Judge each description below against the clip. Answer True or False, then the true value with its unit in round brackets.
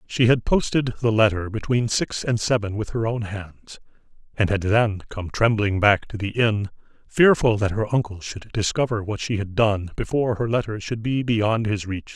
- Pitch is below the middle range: True (110 Hz)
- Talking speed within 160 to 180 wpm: False (195 wpm)